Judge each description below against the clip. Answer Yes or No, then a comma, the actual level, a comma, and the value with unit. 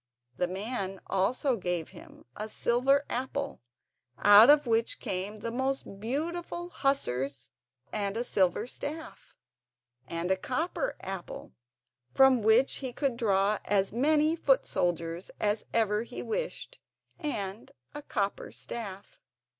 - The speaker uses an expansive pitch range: Yes, wide, 6.0 semitones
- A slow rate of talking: Yes, slow, 130 wpm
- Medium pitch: No, high, 230 Hz